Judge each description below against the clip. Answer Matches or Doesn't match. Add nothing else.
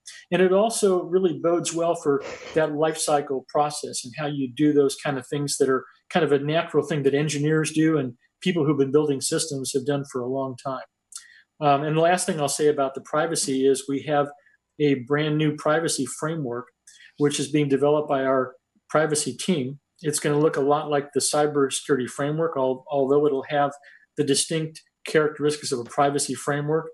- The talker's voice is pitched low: Doesn't match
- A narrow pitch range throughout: Matches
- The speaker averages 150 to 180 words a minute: Doesn't match